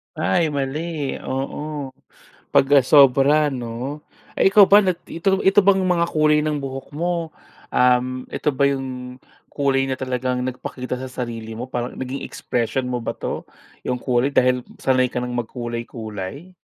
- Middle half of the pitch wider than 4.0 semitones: No, average, 3.2 semitones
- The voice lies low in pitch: Yes, low, 130 Hz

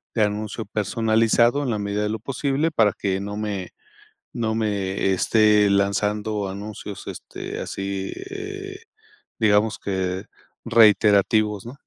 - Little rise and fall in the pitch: Yes, narrow, 2.2 semitones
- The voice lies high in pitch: No, low, 105 Hz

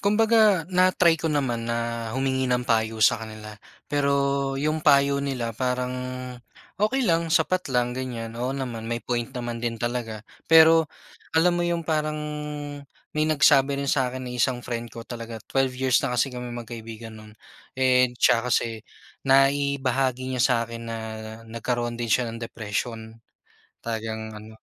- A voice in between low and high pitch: No, low, 125 Hz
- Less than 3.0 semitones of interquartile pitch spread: No, average, 3.3 semitones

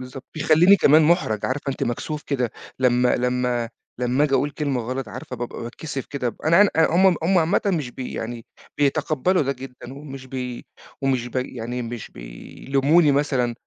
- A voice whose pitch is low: Yes, low, 130 Hz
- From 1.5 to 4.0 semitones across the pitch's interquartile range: Yes, average, 3.6 semitones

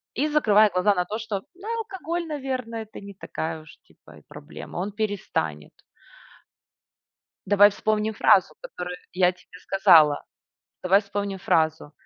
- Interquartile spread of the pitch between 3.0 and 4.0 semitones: Yes, average, 3.7 semitones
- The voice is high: Yes, high, 200 Hz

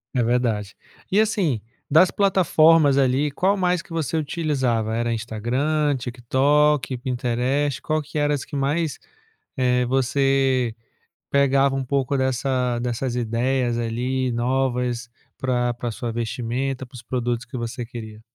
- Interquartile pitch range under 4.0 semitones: Yes, average, 3.0 semitones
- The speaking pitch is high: No, low, 130 Hz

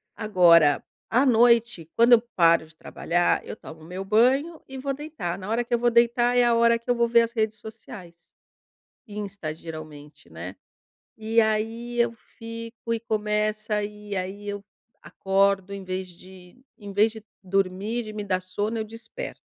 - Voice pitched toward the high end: Yes, high, 215 Hz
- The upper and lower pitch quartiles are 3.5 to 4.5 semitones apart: Yes, average, 3.9 semitones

